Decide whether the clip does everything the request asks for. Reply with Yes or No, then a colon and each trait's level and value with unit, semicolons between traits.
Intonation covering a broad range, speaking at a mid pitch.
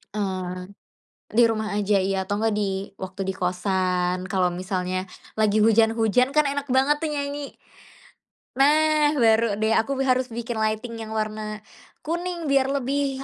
No: wide, 5.9 semitones; high, 220 Hz